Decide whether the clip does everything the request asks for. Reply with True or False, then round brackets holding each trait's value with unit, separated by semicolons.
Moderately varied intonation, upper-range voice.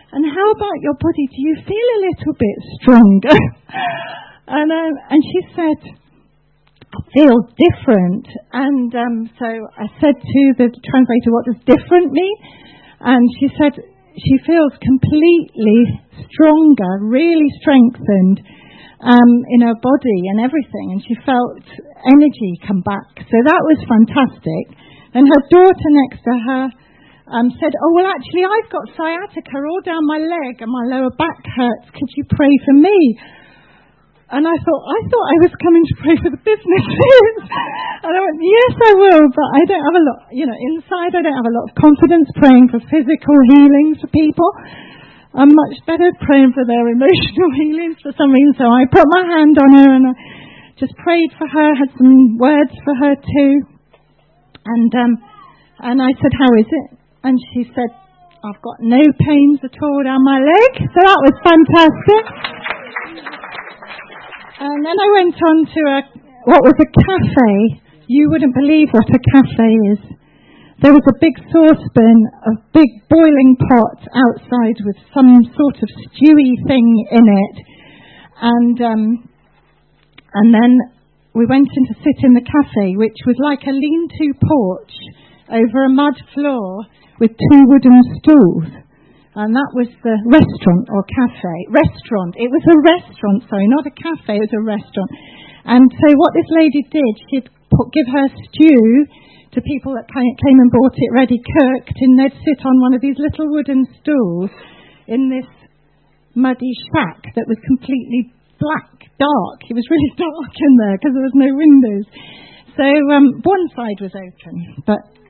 True (4.4 semitones; 270 Hz)